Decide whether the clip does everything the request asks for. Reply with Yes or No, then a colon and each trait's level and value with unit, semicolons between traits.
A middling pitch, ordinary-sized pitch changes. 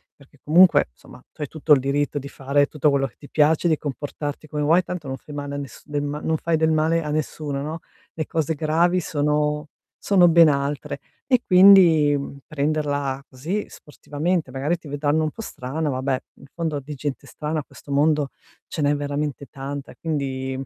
No: medium, 150 Hz; narrow, 2.1 semitones